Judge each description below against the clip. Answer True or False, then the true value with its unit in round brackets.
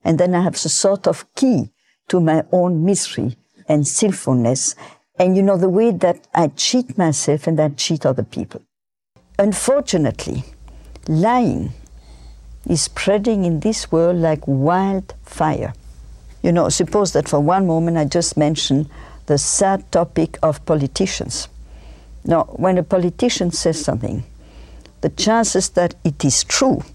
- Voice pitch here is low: False (165 Hz)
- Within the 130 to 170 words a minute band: True (145 wpm)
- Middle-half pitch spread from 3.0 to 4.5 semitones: False (5.2 semitones)